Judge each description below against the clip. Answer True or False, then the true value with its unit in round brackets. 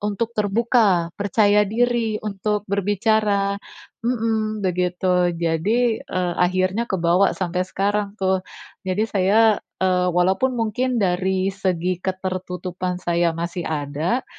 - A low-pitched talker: False (190 Hz)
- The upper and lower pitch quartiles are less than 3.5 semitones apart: True (3.0 semitones)